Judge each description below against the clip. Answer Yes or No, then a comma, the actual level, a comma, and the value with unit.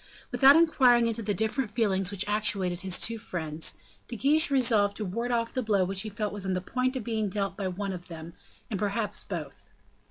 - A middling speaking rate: No, fast, 220 wpm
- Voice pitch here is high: Yes, high, 210 Hz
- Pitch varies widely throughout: No, average, 3.4 semitones